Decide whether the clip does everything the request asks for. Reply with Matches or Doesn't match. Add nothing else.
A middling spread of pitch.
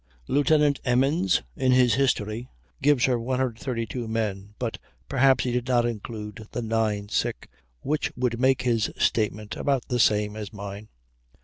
Matches